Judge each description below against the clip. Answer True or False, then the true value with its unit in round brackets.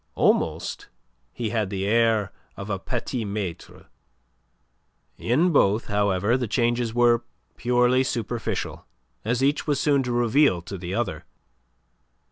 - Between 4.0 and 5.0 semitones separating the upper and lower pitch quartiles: False (3.3 semitones)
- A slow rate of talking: True (125 wpm)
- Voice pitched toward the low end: True (115 Hz)